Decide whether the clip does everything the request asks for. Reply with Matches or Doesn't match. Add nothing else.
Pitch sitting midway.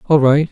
Matches